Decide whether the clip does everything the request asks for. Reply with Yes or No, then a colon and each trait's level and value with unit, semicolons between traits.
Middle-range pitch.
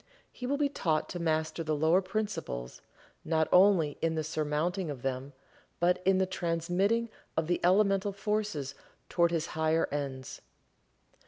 Yes: medium, 165 Hz